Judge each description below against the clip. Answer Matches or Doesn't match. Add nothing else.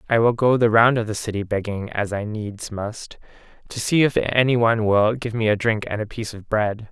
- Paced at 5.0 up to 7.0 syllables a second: Matches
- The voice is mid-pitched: Doesn't match